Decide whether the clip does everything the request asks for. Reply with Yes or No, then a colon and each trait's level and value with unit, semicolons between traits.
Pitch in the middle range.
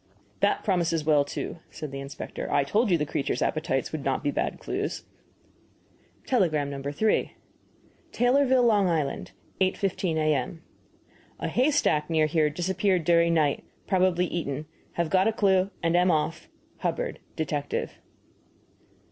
Yes: medium, 165 Hz